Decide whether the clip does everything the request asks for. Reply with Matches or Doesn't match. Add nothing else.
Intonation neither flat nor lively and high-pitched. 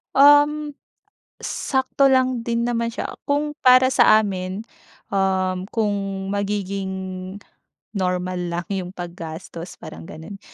Doesn't match